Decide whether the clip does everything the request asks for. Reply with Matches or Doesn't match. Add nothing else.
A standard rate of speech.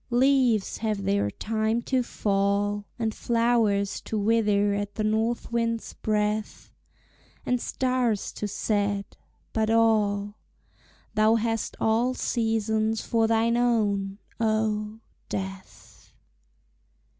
Doesn't match